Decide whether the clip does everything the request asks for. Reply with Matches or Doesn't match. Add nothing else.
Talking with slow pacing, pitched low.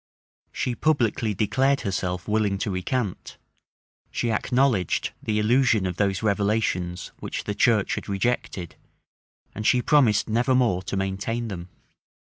Matches